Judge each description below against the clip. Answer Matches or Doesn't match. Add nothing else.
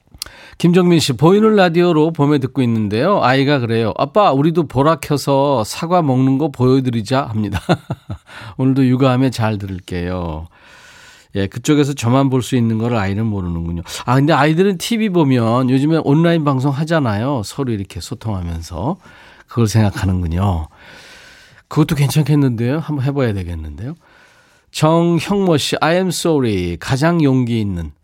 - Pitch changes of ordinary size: Doesn't match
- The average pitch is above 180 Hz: Doesn't match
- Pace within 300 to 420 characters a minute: Matches